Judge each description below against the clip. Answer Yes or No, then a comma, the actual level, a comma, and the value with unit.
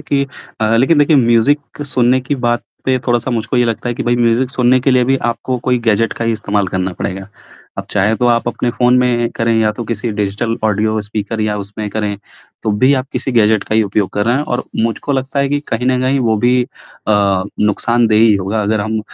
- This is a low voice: Yes, low, 115 Hz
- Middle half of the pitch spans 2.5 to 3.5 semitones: Yes, average, 2.8 semitones